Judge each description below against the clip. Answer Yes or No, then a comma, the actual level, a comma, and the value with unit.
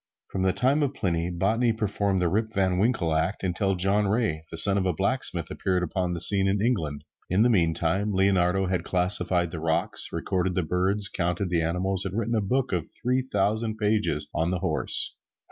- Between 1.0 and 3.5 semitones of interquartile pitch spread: Yes, average, 3.1 semitones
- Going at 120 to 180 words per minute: No, average, 195 wpm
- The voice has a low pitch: Yes, very low, 95 Hz